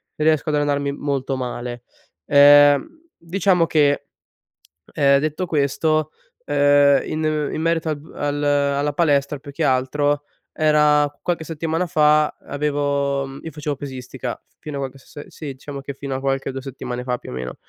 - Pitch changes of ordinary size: No, narrow, 1.8 semitones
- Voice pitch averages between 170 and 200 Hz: No, medium, 145 Hz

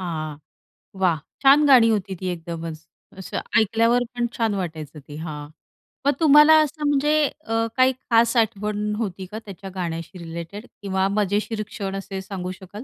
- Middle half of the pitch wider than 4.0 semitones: Yes, average, 4.7 semitones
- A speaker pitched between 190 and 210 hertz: Yes, high, 200 Hz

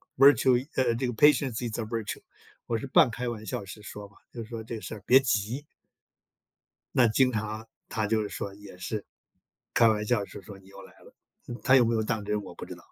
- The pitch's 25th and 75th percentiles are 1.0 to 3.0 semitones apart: Yes, average, 2.7 semitones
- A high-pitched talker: No, low, 110 Hz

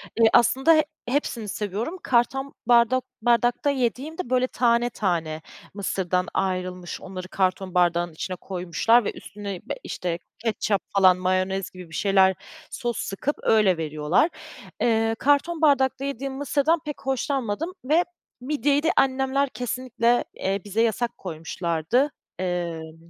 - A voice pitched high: Yes, high, 225 Hz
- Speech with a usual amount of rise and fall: No, wide, 6.4 semitones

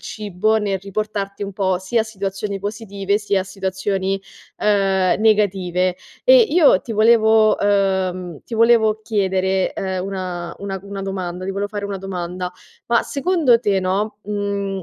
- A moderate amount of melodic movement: No, narrow, 2.1 semitones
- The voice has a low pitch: No, high, 200 Hz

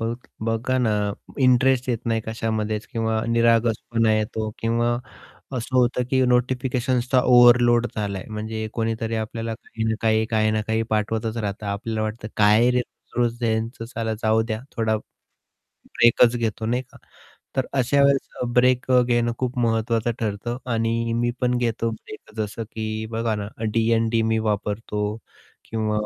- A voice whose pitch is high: No, low, 115 Hz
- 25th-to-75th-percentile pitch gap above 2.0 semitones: No, narrow, 1.6 semitones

